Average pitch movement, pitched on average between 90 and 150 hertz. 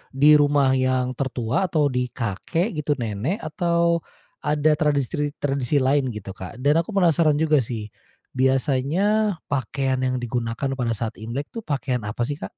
Yes: average, 3.6 semitones; medium, 140 Hz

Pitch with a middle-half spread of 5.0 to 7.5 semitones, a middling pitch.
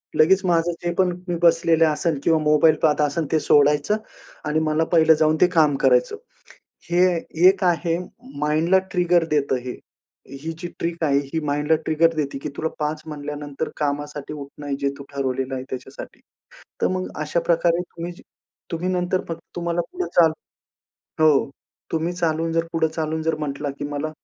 No: narrow, 2.4 semitones; medium, 160 Hz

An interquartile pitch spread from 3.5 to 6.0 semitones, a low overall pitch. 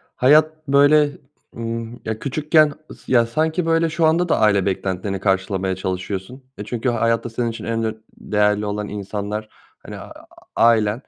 Yes: wide, 5.6 semitones; low, 115 Hz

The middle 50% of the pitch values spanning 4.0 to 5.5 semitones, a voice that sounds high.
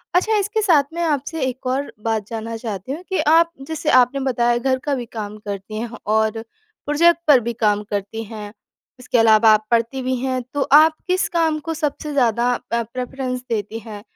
Yes: average, 4.9 semitones; very high, 250 Hz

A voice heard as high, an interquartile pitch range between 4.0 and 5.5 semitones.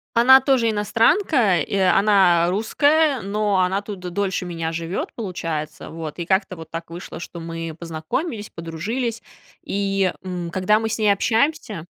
Yes: high, 195 Hz; average, 4.7 semitones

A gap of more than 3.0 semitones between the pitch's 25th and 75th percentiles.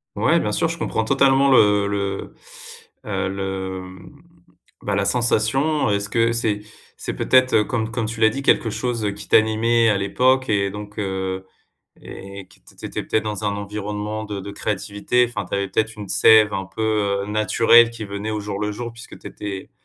No: narrow, 2.4 semitones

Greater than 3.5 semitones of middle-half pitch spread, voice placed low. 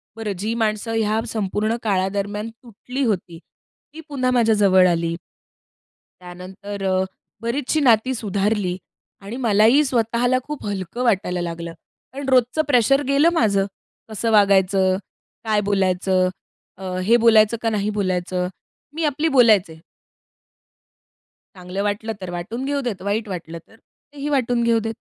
No: average, 3.9 semitones; high, 215 Hz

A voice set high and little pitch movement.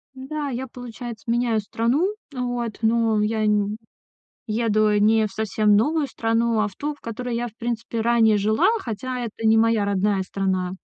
Yes: high, 225 Hz; narrow, 2.2 semitones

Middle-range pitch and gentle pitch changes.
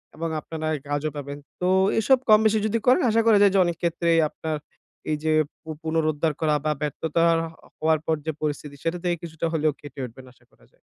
Yes: medium, 160 Hz; narrow, 2.3 semitones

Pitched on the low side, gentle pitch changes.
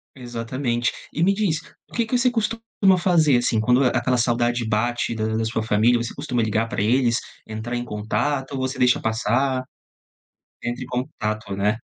No: low, 120 Hz; average, 3.3 semitones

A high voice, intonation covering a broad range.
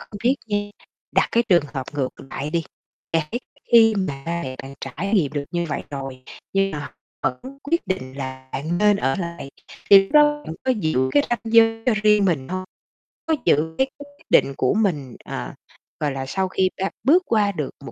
No: medium, 175 Hz; wide, 7.3 semitones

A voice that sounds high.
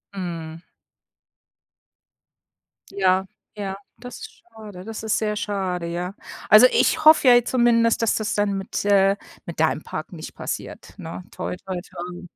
Yes: high, 200 Hz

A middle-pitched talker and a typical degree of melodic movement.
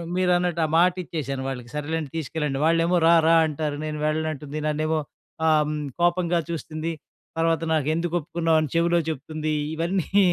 No: medium, 160 Hz; narrow, 1.8 semitones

